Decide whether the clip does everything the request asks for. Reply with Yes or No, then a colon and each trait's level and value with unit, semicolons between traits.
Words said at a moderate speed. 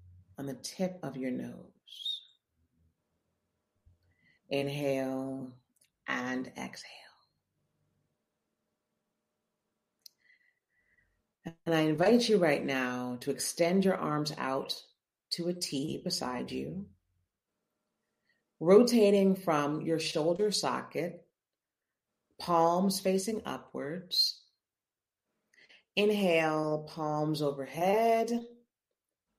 No: slow, 75 wpm